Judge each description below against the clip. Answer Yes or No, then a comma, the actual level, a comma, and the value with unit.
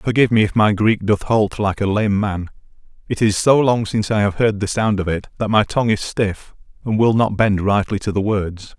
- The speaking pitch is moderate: No, low, 105 Hz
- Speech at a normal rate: No, fast, 245 wpm